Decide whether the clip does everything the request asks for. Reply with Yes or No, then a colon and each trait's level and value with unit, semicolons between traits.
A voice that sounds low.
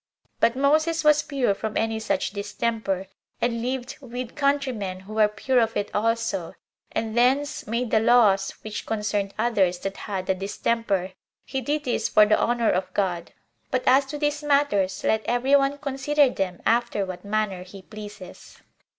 No: high, 225 Hz